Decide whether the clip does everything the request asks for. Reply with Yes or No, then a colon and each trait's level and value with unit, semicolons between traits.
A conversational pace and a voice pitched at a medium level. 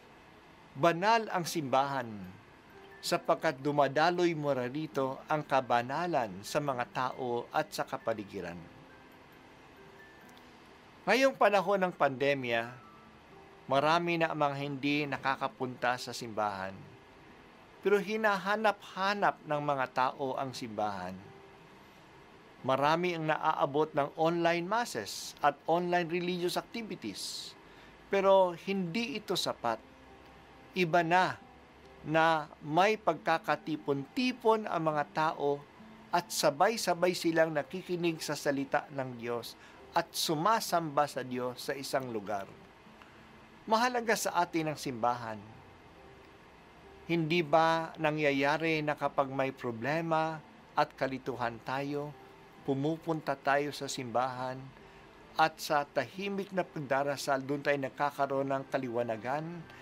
No: slow, 100 wpm; medium, 145 Hz